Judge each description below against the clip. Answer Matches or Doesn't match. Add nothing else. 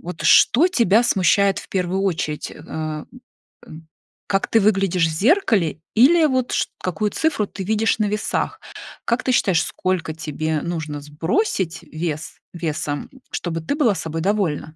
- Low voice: Doesn't match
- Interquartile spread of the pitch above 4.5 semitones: Matches